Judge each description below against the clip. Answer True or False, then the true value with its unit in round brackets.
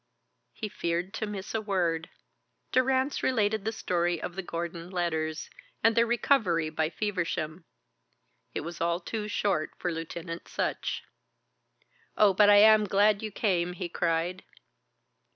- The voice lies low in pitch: False (185 Hz)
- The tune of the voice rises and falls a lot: False (4.0 semitones)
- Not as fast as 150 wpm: True (140 wpm)